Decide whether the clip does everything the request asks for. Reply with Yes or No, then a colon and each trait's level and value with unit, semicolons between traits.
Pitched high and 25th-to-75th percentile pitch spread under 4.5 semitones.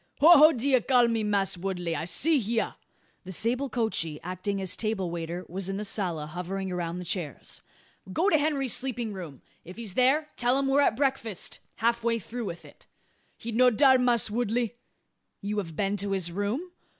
No: high, 215 Hz; average, 5.3 semitones